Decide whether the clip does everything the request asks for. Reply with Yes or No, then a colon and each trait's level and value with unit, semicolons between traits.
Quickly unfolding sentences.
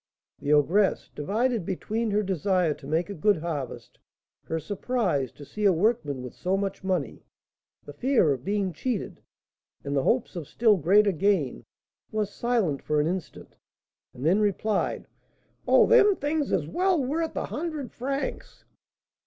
No: average, 155 wpm